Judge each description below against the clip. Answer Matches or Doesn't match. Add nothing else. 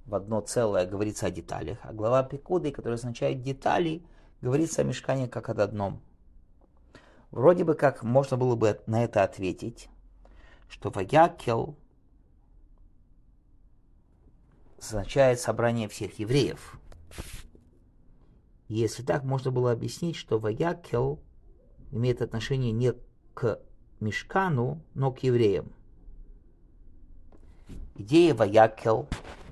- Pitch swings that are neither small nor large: Doesn't match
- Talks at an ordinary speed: Doesn't match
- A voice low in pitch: Matches